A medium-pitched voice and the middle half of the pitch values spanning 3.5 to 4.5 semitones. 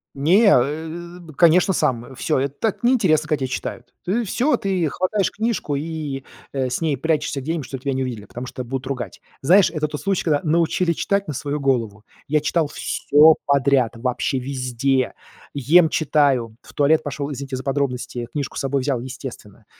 Yes: medium, 145 Hz; average, 3.9 semitones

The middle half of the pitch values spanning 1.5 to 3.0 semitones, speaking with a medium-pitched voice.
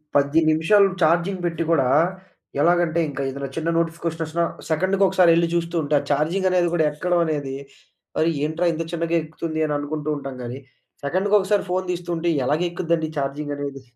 Yes: narrow, 2.6 semitones; medium, 165 Hz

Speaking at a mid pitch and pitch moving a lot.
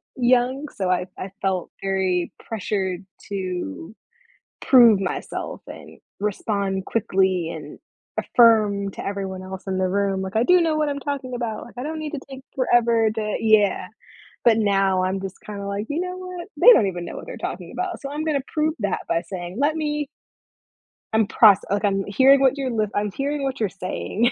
No: high, 210 Hz; wide, 5.8 semitones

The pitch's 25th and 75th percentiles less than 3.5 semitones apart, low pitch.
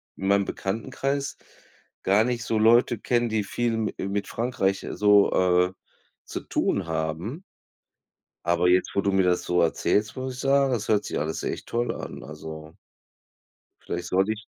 No: average, 4.8 semitones; low, 100 Hz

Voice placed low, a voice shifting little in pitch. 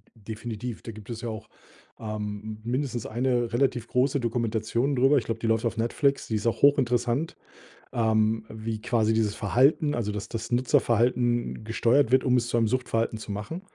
Yes: low, 115 Hz; narrow, 2.2 semitones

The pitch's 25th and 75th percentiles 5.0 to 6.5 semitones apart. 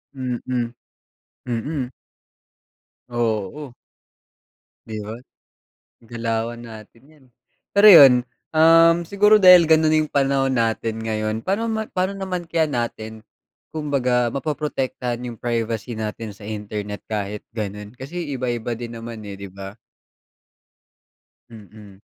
Yes: wide, 5.6 semitones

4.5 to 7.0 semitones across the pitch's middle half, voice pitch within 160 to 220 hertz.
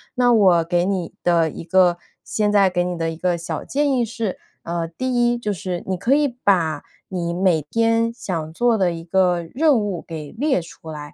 Yes: average, 5.1 semitones; medium, 185 Hz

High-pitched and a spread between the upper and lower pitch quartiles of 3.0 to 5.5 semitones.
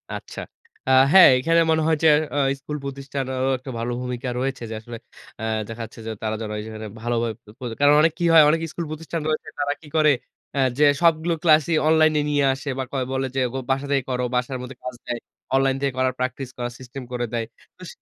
No: low, 135 Hz; average, 3.5 semitones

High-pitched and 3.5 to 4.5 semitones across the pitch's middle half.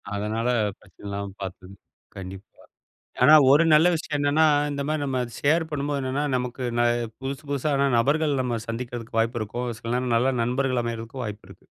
No: low, 125 Hz; average, 3.8 semitones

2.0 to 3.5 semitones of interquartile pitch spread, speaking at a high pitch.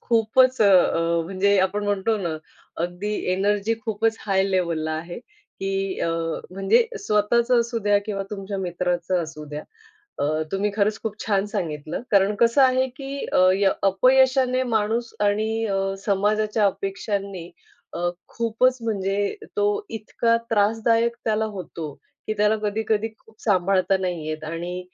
Yes: average, 3.2 semitones; high, 205 Hz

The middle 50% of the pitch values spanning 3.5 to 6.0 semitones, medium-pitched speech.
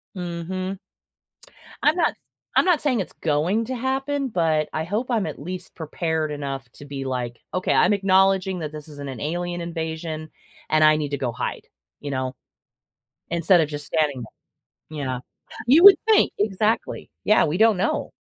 Yes: average, 4.9 semitones; medium, 165 Hz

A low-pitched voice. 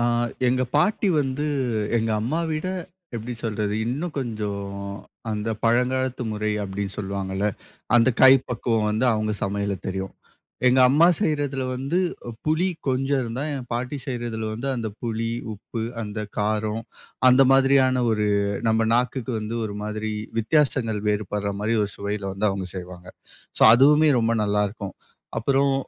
Yes: low, 115 Hz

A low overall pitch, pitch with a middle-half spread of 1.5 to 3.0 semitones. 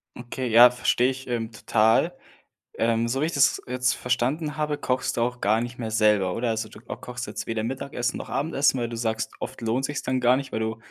Yes: low, 120 Hz; average, 2.7 semitones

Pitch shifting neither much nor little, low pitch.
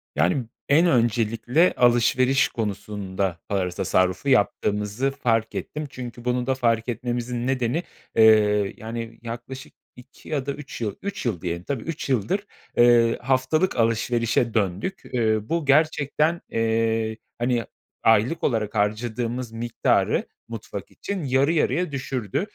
Yes: average, 3.3 semitones; low, 120 Hz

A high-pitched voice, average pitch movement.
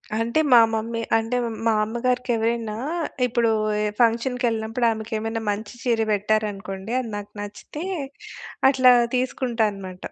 No: high, 225 Hz; narrow, 1.9 semitones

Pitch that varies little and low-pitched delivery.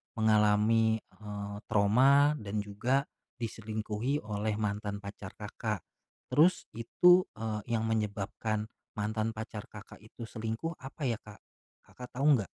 Yes: narrow, 2.0 semitones; low, 110 Hz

